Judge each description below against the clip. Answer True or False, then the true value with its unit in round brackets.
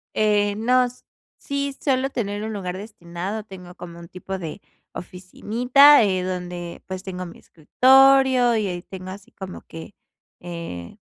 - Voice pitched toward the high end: True (195 Hz)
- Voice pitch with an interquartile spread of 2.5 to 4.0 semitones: False (5.2 semitones)